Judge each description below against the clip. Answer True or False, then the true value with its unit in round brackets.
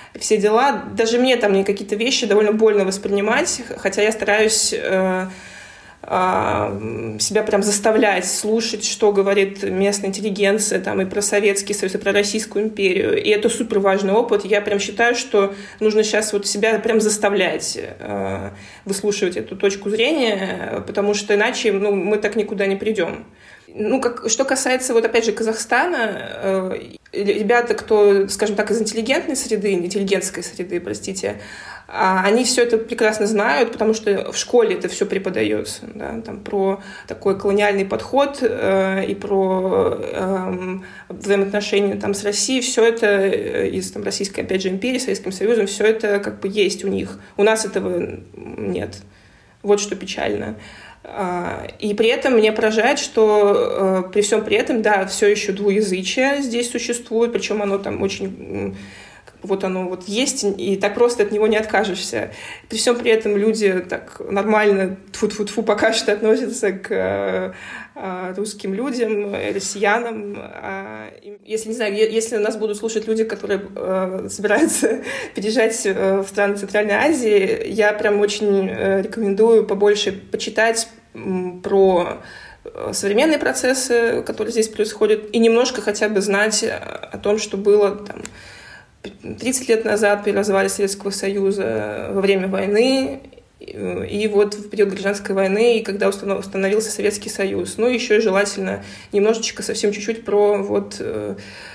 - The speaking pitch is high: True (205 Hz)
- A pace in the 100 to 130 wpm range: False (145 wpm)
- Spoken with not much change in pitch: True (2.2 semitones)